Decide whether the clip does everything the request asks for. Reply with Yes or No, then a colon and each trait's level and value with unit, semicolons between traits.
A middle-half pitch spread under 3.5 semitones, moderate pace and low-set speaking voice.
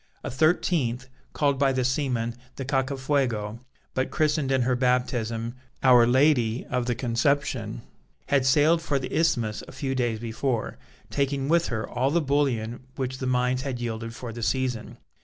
Yes: average, 2.8 semitones; average, 160 wpm; low, 130 Hz